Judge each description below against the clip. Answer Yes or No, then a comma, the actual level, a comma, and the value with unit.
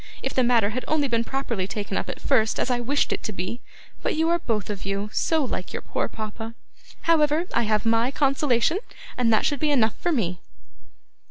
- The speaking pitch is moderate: No, high, 235 Hz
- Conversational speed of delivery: No, fast, 210 wpm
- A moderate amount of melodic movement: Yes, average, 4.9 semitones